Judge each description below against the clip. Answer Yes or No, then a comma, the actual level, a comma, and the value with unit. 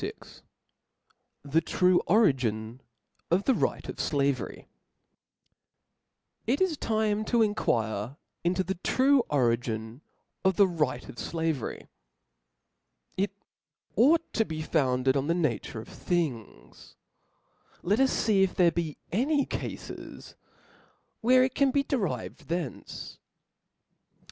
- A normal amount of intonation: No, wide, 8.5 semitones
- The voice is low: No, medium, 175 Hz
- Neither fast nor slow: No, slow, 125 wpm